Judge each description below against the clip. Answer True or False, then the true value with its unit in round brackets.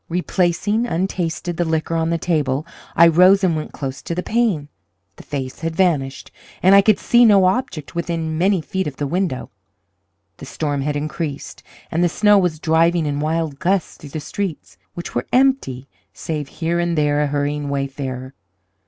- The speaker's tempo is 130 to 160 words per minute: False (180 wpm)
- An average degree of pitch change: True (3.8 semitones)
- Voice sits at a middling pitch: True (165 Hz)